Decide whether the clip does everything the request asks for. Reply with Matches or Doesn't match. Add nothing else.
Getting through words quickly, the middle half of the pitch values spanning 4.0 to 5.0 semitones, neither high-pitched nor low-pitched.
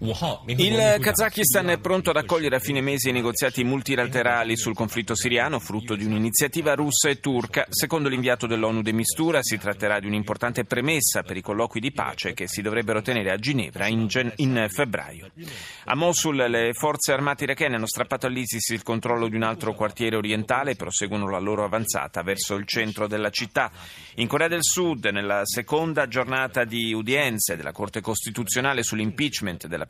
Doesn't match